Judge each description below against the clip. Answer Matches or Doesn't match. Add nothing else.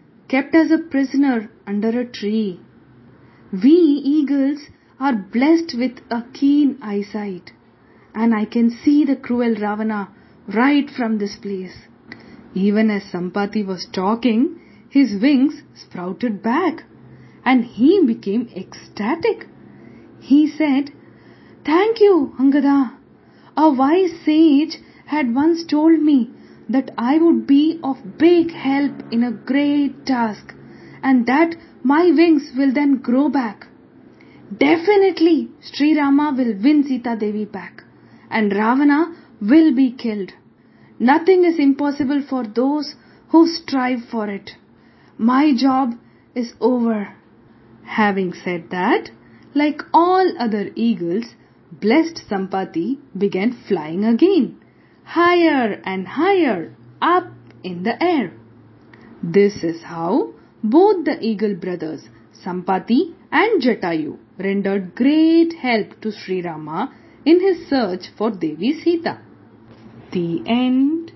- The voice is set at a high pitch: Matches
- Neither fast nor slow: Doesn't match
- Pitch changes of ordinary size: Doesn't match